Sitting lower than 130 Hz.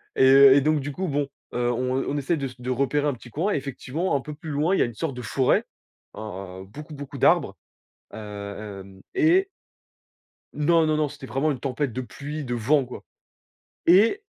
No: medium, 140 Hz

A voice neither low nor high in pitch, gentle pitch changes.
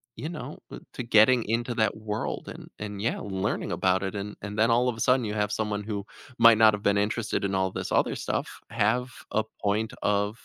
No: low, 110 Hz; narrow, 2.3 semitones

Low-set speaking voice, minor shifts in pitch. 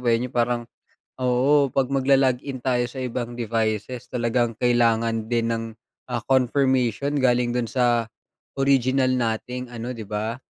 Yes: low, 125 Hz; narrow, 1.9 semitones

